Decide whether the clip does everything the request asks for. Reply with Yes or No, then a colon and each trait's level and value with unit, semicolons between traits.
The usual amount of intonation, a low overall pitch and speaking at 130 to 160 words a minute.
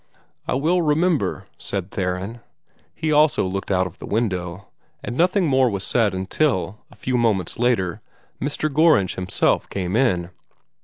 No: wide, 7.9 semitones; low, 110 Hz; average, 150 wpm